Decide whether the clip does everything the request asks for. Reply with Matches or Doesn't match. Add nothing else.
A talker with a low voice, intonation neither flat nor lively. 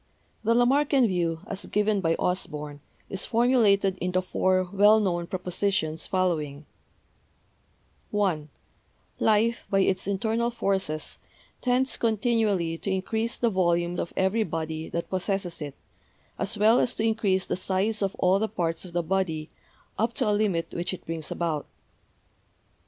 Doesn't match